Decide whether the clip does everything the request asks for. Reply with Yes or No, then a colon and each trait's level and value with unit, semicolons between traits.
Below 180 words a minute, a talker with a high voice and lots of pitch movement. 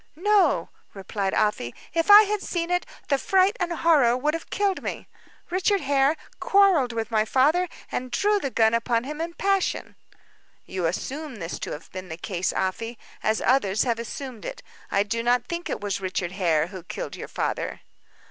No: average, 185 wpm; very high, 255 Hz; wide, 8.8 semitones